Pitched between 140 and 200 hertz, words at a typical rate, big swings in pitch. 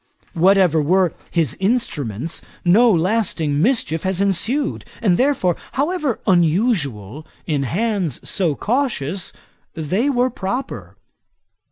No: medium, 185 Hz; slow, 100 wpm; wide, 6.5 semitones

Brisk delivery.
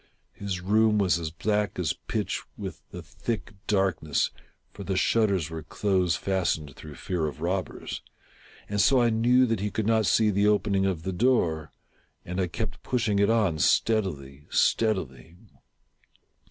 No: average, 155 wpm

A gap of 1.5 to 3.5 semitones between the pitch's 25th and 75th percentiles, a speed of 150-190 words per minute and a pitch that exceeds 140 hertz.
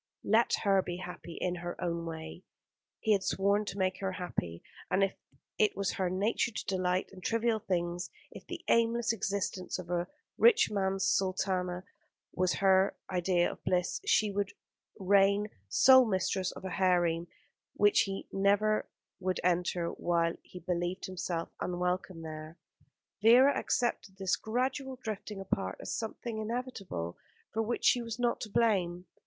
Yes: average, 3.2 semitones; average, 155 wpm; high, 190 Hz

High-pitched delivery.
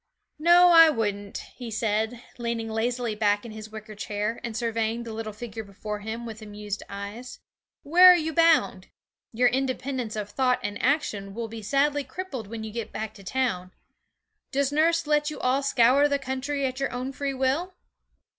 Yes: high, 235 Hz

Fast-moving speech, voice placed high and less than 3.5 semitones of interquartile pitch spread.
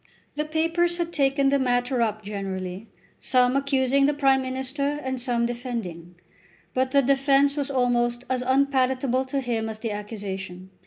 No: average, 155 wpm; very high, 260 Hz; average, 3.1 semitones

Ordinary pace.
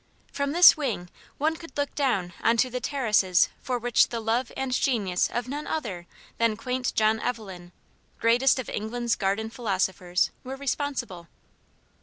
Yes: average, 155 wpm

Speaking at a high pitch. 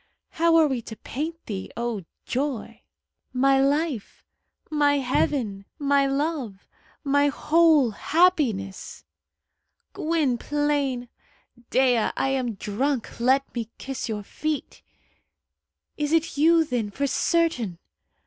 Yes: very high, 275 Hz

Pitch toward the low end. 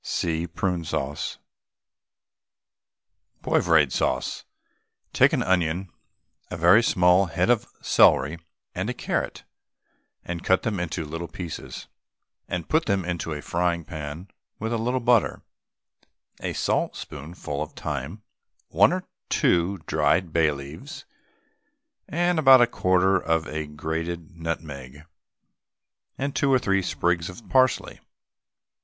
Yes: very low, 85 Hz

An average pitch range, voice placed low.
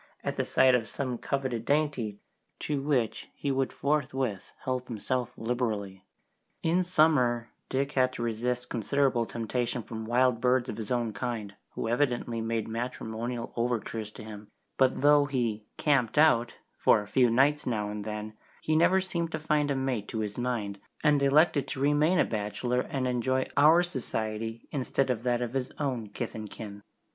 Yes: average, 3.6 semitones; low, 125 Hz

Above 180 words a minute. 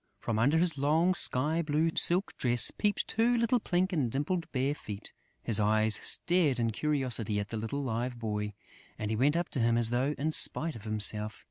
Yes: average, 200 wpm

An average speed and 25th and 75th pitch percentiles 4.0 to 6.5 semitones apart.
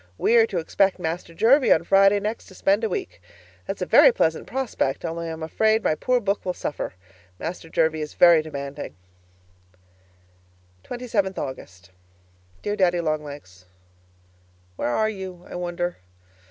Yes: average, 155 wpm; average, 4.6 semitones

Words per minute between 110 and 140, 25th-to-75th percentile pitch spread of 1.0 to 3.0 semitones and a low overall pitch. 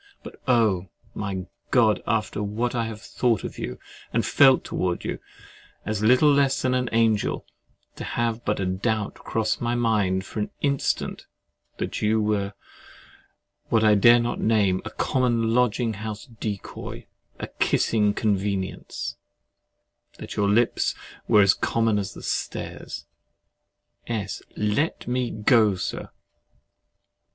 Yes: slow, 135 wpm; narrow, 2.5 semitones; low, 110 Hz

